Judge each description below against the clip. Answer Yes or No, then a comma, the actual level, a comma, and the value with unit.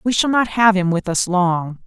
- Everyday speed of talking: No, fast, 255 wpm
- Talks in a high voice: Yes, high, 195 Hz